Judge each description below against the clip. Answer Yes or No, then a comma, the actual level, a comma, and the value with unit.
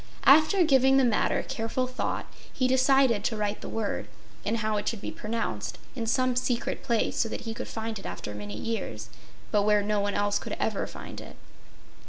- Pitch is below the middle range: No, high, 225 Hz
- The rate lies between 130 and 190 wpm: No, average, 200 wpm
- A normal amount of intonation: Yes, average, 3.4 semitones